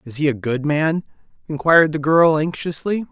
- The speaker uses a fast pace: No, average, 175 wpm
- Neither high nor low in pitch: Yes, medium, 150 Hz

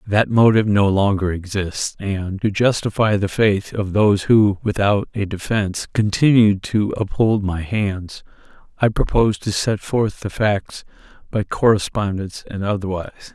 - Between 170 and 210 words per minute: No, average, 145 wpm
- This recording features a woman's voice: No, male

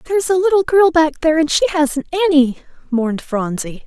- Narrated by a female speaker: Yes, female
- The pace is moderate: Yes, average, 185 wpm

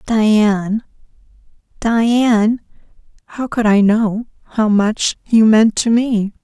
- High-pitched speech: Yes, high, 220 Hz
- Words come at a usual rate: No, slow, 110 wpm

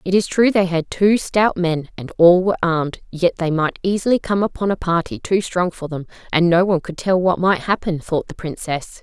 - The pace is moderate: No, fast, 235 wpm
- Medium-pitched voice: Yes, medium, 180 Hz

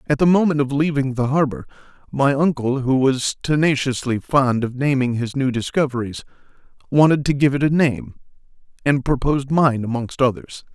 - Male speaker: Yes, male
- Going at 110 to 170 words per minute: Yes, average, 160 wpm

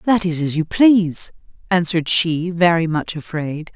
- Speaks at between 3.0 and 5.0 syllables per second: Yes, 4.6 syllables/s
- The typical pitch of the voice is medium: Yes, medium, 170 Hz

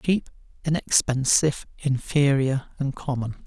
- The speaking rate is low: Yes, slow, 85 wpm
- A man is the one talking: Yes, male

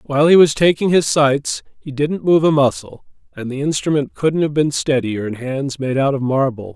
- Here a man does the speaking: Yes, male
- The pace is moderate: No, fast, 215 wpm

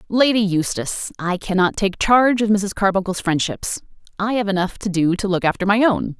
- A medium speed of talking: Yes, average, 195 wpm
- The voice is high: Yes, high, 200 Hz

